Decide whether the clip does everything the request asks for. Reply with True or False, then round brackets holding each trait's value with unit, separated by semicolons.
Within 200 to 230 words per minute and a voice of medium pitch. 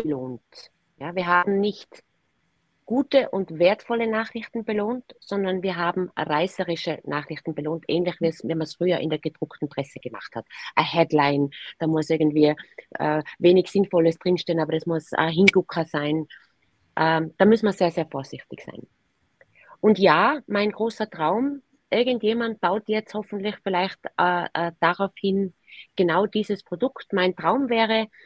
False (145 wpm; 180 Hz)